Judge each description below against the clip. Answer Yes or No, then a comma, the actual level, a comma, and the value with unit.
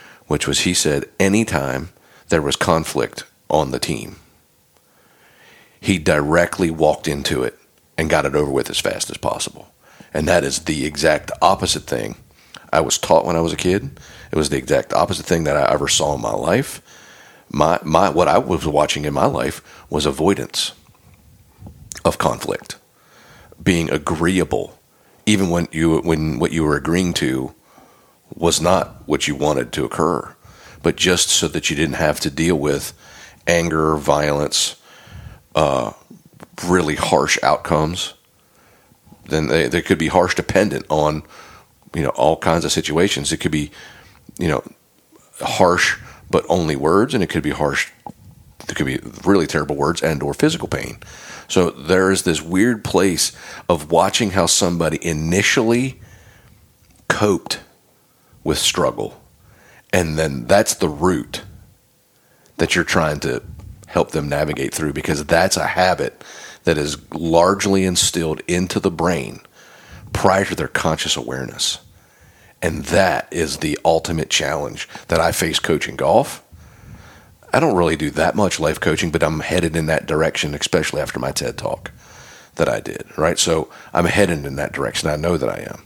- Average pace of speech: Yes, average, 160 wpm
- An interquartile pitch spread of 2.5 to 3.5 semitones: Yes, average, 3.0 semitones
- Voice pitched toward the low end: Yes, very low, 85 Hz